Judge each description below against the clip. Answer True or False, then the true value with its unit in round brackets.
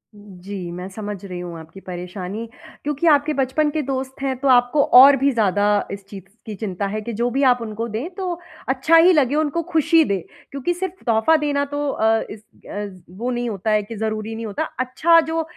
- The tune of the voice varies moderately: False (6.0 semitones)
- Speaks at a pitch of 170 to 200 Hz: False (235 Hz)